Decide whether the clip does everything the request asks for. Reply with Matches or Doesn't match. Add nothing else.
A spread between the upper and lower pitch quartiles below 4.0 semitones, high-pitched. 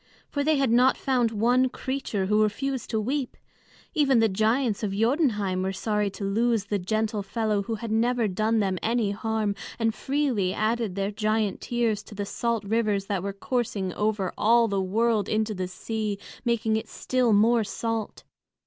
Matches